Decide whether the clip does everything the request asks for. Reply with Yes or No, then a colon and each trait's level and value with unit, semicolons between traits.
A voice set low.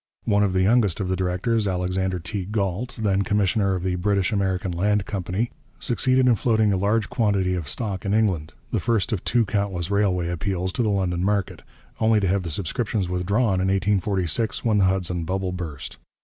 Yes: very low, 95 Hz